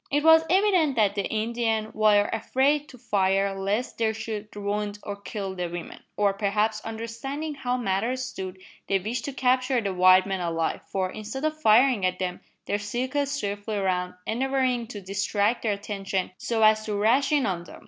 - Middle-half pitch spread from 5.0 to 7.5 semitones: No, average, 4.3 semitones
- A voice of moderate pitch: No, high, 215 Hz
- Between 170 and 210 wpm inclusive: Yes, average, 180 wpm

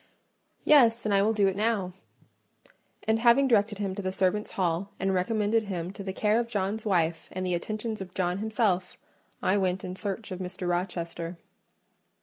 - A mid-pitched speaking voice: No, high, 195 Hz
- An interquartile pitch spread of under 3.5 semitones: Yes, average, 2.9 semitones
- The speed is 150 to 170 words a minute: No, average, 180 wpm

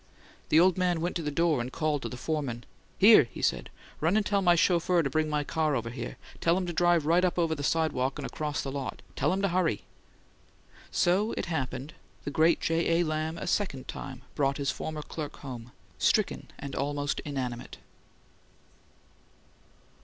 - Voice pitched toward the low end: No, medium, 155 Hz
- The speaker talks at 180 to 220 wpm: Yes, average, 190 wpm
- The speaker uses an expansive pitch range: No, average, 3.8 semitones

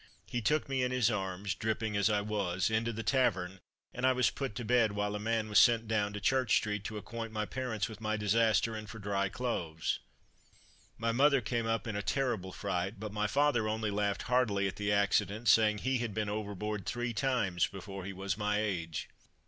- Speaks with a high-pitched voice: No, low, 105 Hz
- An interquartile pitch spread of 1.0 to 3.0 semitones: Yes, narrow, 2.4 semitones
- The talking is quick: Yes, fast, 210 wpm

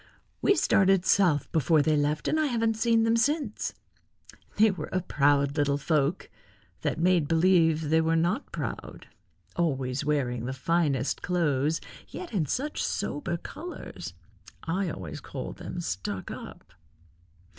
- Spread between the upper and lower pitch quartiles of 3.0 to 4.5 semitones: No, average, 5.2 semitones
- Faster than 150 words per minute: No, average, 140 wpm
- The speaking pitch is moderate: Yes, medium, 165 Hz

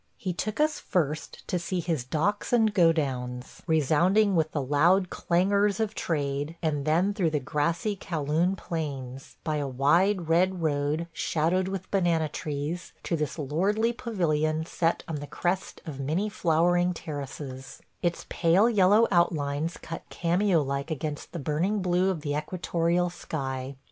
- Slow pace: No, average, 155 wpm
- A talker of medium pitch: Yes, medium, 165 Hz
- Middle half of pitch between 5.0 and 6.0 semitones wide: No, average, 3.9 semitones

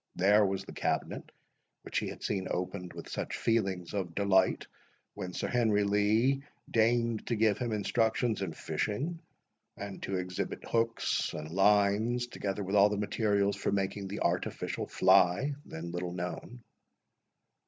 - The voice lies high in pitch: No, low, 100 Hz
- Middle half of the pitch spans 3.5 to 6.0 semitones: No, average, 3.0 semitones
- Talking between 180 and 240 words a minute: No, average, 150 wpm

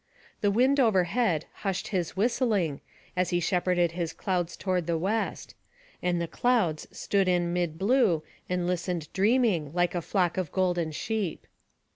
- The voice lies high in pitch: No, medium, 180 Hz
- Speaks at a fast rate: No, average, 150 wpm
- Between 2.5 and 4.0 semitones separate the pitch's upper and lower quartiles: Yes, average, 2.9 semitones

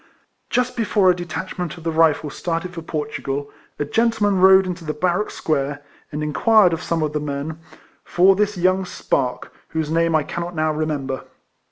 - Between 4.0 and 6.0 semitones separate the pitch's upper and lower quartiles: No, average, 3.5 semitones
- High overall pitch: No, medium, 165 Hz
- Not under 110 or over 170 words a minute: No, average, 180 wpm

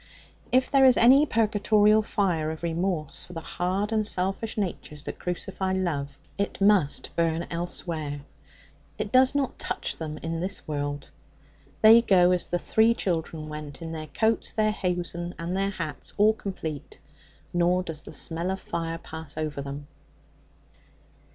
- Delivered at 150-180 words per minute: Yes, average, 155 wpm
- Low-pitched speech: No, medium, 175 Hz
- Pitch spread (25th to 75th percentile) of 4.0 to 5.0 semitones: Yes, average, 4.4 semitones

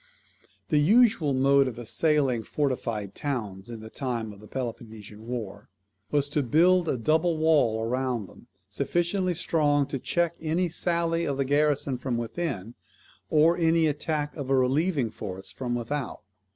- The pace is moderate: Yes, average, 150 wpm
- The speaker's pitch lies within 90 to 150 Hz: Yes, medium, 140 Hz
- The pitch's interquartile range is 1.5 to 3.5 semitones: No, average, 5.2 semitones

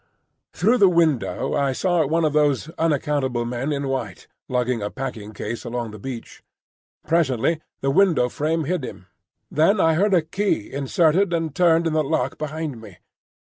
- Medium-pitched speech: Yes, medium, 150 Hz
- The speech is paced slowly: No, average, 170 wpm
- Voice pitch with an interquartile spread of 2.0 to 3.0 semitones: No, average, 4.8 semitones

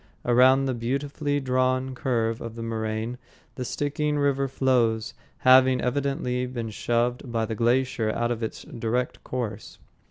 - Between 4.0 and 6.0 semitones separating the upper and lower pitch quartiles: No, narrow, 2.4 semitones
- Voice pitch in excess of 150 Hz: No, low, 125 Hz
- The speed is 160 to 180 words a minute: No, average, 140 wpm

